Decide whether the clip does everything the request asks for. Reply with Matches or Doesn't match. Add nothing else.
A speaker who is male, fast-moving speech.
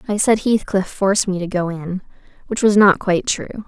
Doesn't match